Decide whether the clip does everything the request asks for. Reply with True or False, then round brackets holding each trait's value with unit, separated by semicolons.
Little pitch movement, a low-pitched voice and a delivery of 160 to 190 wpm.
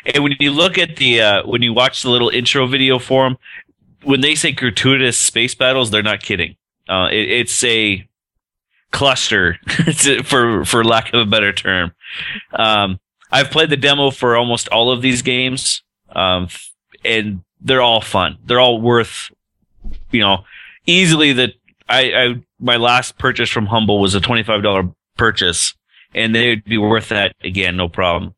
False (3.7 semitones; 120 Hz; 170 wpm)